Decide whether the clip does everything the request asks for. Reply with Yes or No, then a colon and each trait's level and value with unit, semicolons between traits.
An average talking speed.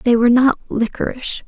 Yes: average, 165 wpm